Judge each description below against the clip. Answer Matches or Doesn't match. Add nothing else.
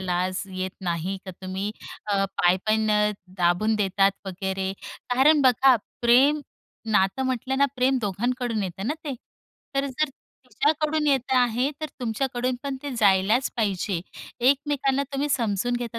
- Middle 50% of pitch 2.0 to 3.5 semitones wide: Doesn't match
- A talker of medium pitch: Doesn't match